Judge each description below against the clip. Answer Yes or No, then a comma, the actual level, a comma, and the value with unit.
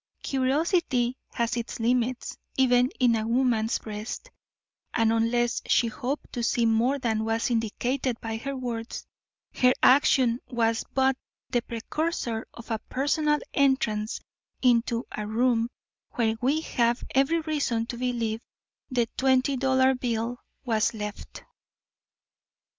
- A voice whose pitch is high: Yes, high, 240 Hz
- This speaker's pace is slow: Yes, slow, 125 wpm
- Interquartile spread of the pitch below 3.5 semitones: Yes, narrow, 2.5 semitones